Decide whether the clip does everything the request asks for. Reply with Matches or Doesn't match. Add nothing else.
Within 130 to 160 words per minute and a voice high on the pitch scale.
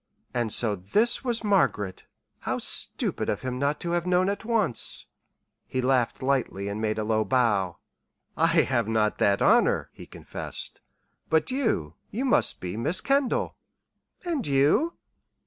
Doesn't match